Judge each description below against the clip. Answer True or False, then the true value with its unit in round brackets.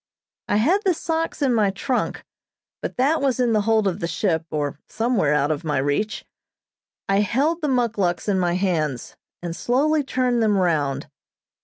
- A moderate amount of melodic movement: False (7.2 semitones)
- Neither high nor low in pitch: False (210 Hz)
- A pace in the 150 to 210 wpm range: True (175 wpm)